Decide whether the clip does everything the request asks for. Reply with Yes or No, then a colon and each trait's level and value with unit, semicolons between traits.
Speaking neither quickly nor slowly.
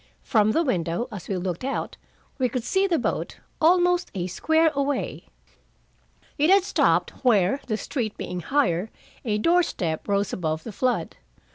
Yes: average, 160 wpm